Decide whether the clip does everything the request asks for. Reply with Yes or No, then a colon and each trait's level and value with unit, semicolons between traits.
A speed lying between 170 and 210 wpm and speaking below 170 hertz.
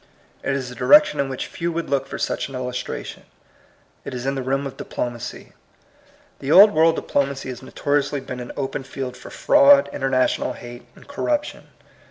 Yes: average, 185 wpm; low, 135 Hz